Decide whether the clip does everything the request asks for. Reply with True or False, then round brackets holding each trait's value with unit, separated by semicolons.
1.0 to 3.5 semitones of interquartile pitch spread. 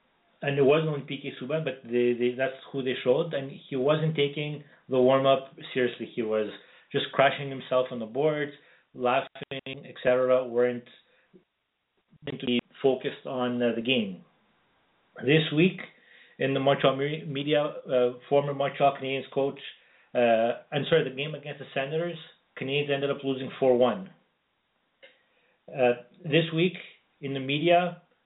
True (2.6 semitones)